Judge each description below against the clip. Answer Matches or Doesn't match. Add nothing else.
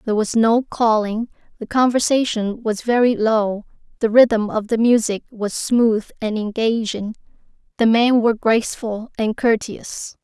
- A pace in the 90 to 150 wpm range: Matches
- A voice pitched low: Doesn't match